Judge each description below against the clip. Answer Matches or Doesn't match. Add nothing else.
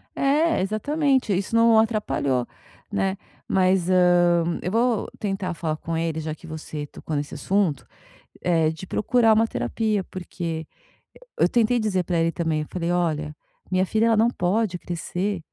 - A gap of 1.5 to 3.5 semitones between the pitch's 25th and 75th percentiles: Doesn't match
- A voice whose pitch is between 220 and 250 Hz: Doesn't match